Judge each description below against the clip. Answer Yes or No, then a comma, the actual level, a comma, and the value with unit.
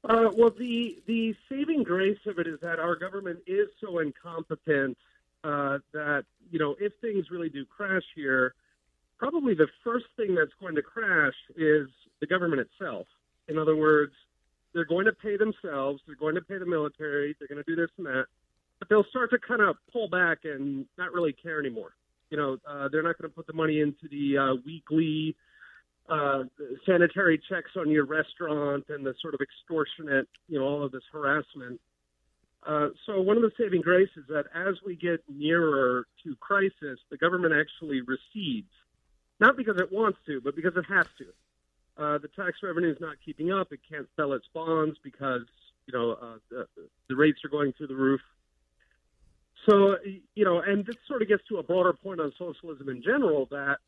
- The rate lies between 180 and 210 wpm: Yes, average, 190 wpm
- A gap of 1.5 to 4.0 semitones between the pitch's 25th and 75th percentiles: No, average, 5.1 semitones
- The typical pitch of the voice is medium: Yes, medium, 155 Hz